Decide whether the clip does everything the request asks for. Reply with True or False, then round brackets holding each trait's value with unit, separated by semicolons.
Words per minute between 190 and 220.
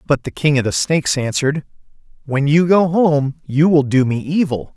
True (200 wpm)